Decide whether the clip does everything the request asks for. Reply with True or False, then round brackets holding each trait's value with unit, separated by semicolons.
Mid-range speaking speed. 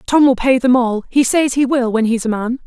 False (295 wpm)